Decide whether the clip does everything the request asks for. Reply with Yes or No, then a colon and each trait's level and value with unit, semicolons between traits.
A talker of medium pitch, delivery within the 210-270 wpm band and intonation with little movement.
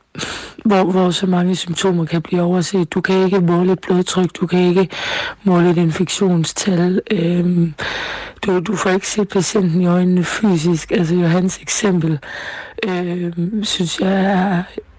No: medium, 180 Hz; average, 150 wpm; narrow, 1.6 semitones